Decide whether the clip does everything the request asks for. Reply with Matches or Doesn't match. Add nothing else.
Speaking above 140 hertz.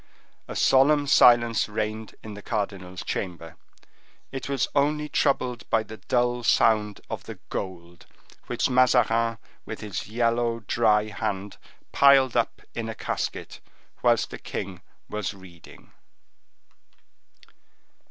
Doesn't match